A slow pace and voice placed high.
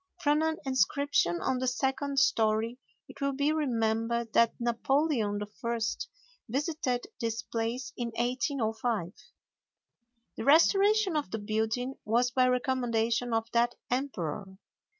Yes: slow, 120 wpm; high, 245 Hz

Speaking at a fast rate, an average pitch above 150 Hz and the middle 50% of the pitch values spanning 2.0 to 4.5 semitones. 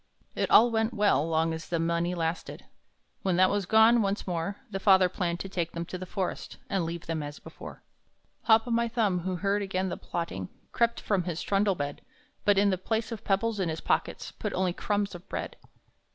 Yes: fast, 210 wpm; high, 190 Hz; average, 3.2 semitones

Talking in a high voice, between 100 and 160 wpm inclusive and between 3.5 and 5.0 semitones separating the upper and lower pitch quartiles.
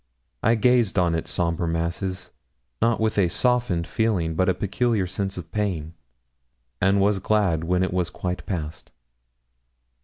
No: very low, 95 Hz; average, 150 wpm; average, 3.8 semitones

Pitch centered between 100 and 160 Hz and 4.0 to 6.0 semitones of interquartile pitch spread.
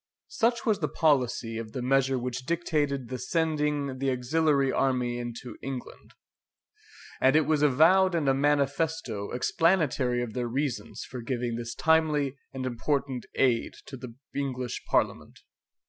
No: low, 135 Hz; average, 3.5 semitones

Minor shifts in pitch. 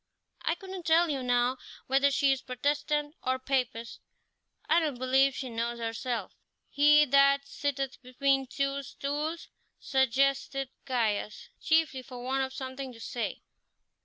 Yes: narrow, 2.0 semitones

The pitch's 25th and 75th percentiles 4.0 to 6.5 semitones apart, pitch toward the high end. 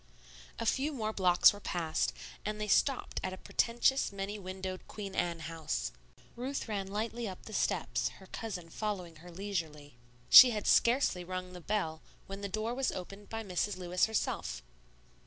No: average, 3.4 semitones; high, 195 Hz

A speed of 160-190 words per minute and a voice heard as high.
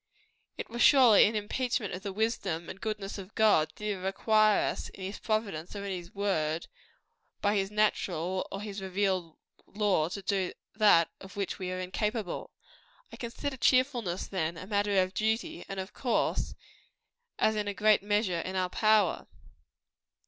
Yes: average, 170 wpm; high, 200 Hz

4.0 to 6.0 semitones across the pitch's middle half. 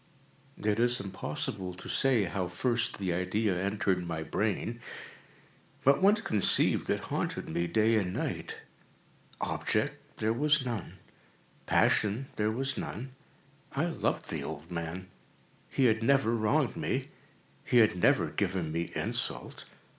Yes: average, 4.7 semitones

